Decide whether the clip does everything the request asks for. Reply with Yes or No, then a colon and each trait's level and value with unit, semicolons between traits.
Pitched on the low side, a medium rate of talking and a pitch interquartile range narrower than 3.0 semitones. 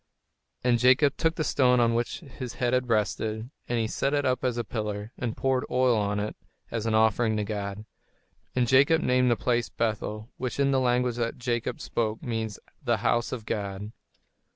Yes: low, 120 Hz; average, 195 wpm; narrow, 2.6 semitones